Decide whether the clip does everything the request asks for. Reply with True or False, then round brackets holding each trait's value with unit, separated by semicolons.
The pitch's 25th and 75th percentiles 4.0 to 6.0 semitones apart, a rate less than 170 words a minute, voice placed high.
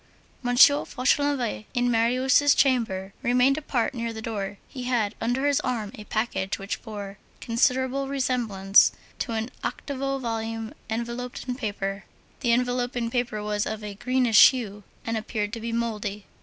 False (3.0 semitones; 150 wpm; 235 Hz)